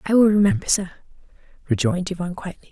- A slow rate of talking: No, average, 155 wpm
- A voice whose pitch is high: Yes, high, 195 Hz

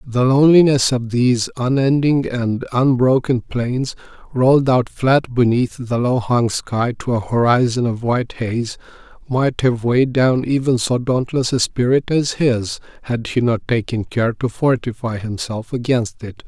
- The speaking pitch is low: Yes, low, 125 Hz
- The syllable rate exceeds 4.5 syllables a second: No, 4.3 syllables/s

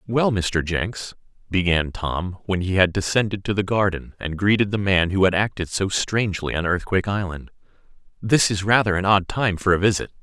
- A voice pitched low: Yes, very low, 95 Hz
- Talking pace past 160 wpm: Yes, average, 195 wpm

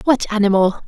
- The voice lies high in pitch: Yes, high, 215 Hz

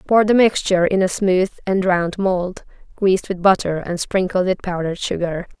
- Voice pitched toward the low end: No, medium, 185 Hz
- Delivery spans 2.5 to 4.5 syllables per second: No, 5.0 syllables/s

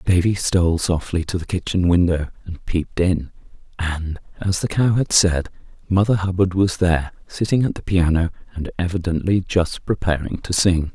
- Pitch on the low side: Yes, very low, 90 Hz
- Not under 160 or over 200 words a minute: Yes, average, 165 wpm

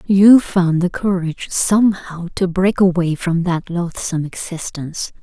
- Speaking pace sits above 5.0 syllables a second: No, 4.4 syllables/s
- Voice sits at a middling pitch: Yes, medium, 180 Hz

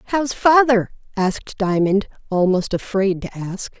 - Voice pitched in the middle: No, high, 210 Hz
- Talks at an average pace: No, slow, 125 wpm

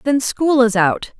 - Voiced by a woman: Yes, female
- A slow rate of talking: No, average, 200 wpm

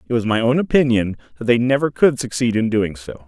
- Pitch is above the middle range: No, low, 120 Hz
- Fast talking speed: Yes, fast, 240 wpm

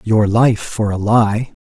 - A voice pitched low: Yes, low, 110 Hz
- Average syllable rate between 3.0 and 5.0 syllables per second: Yes, 3.4 syllables/s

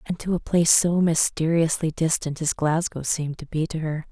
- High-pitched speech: No, medium, 160 Hz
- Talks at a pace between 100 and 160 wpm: No, fast, 205 wpm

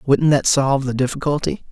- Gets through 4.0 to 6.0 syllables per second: Yes, 5.5 syllables/s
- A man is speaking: Yes, male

